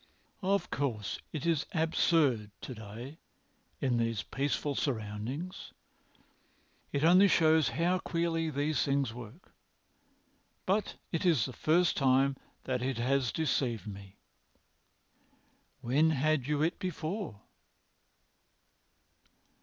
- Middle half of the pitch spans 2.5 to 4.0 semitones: No, average, 5.1 semitones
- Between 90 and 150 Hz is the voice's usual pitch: Yes, medium, 140 Hz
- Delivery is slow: Yes, slow, 105 wpm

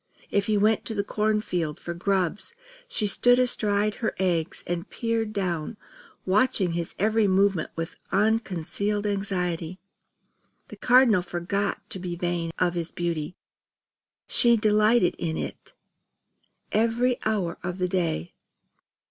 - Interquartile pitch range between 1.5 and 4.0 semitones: Yes, average, 3.7 semitones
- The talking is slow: Yes, slow, 130 wpm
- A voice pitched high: Yes, high, 195 Hz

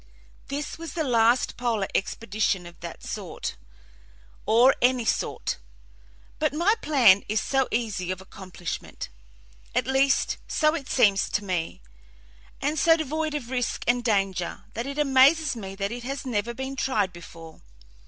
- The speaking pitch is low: No, high, 240 Hz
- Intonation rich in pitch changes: Yes, wide, 5.7 semitones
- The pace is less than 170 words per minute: Yes, average, 150 wpm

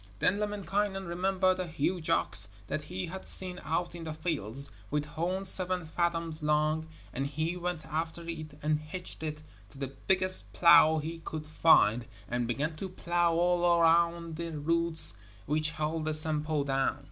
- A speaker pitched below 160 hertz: No, medium, 165 Hz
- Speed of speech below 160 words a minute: No, average, 165 wpm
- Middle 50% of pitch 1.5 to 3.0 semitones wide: Yes, narrow, 2.5 semitones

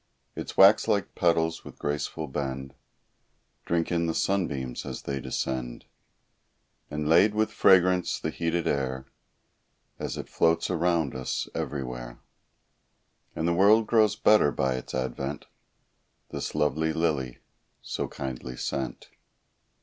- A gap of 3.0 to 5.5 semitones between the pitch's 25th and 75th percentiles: Yes, average, 4.5 semitones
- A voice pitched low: Yes, very low, 80 Hz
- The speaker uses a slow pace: Yes, slow, 125 wpm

